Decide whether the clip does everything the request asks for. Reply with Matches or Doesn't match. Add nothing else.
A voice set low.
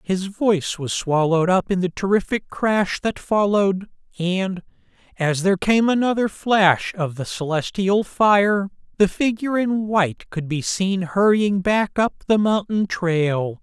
Doesn't match